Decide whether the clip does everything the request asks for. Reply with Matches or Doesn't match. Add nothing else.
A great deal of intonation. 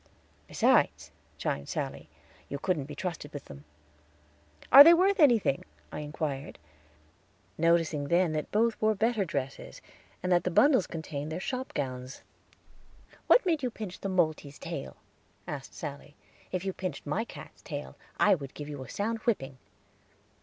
Matches